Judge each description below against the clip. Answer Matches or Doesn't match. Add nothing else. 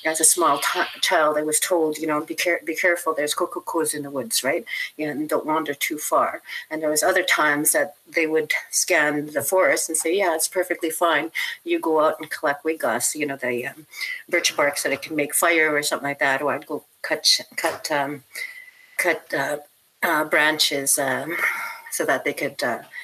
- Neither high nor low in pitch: Matches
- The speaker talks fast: Matches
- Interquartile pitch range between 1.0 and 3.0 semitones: Matches